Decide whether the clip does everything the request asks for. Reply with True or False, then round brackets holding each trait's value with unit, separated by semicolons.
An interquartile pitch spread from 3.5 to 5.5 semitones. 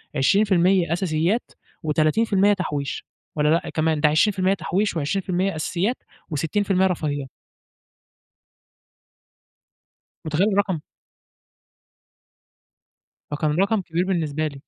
True (4.0 semitones)